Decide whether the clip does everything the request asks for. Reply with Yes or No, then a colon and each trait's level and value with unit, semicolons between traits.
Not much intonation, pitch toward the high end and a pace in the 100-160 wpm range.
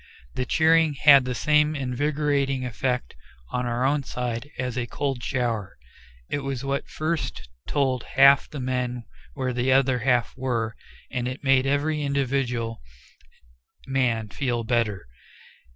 No: narrow, 2.3 semitones; low, 130 Hz; slow, 135 wpm